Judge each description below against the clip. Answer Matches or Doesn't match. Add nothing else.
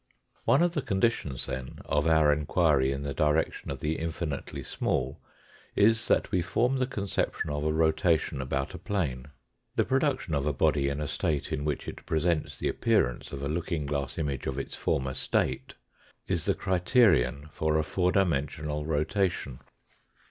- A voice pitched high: Doesn't match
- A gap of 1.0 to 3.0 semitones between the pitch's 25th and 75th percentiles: Doesn't match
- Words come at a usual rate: Matches